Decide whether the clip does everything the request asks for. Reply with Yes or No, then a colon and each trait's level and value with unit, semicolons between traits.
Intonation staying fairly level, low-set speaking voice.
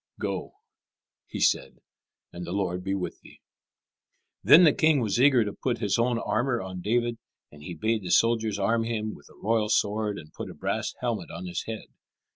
No: average, 3.8 semitones; low, 110 Hz